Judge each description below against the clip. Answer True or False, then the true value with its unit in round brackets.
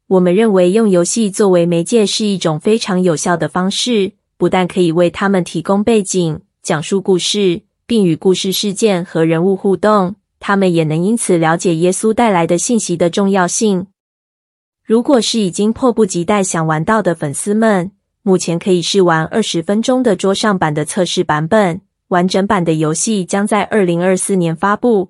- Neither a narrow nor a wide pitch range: True (3.3 semitones)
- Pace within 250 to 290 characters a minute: True (275 characters per minute)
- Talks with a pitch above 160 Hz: True (190 Hz)